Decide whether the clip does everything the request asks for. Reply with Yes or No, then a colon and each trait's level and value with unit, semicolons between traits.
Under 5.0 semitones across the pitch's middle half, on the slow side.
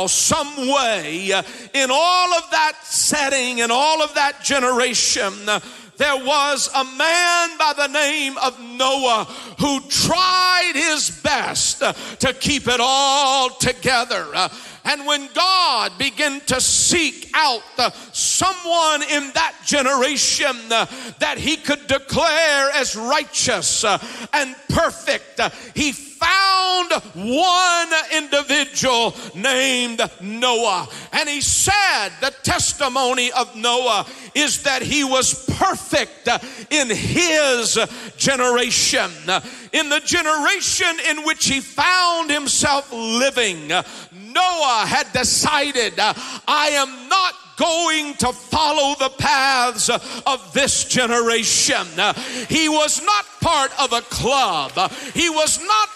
Yes: average, 3.8 semitones; slow, 110 wpm